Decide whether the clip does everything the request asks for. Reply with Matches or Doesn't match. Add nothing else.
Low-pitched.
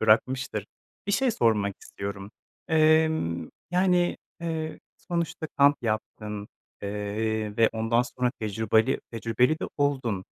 Matches